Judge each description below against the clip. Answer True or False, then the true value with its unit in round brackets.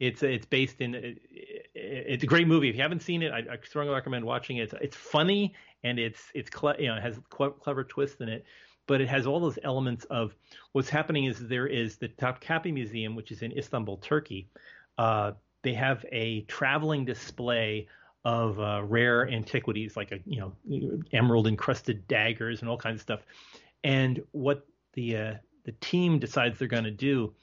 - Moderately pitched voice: False (125 Hz)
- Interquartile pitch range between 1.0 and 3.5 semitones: False (3.9 semitones)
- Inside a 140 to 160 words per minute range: False (190 wpm)